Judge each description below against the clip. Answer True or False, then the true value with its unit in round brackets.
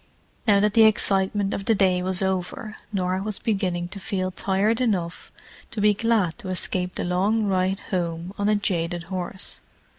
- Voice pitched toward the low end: False (190 Hz)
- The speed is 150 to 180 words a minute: True (175 wpm)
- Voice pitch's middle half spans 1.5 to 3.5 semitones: True (2.5 semitones)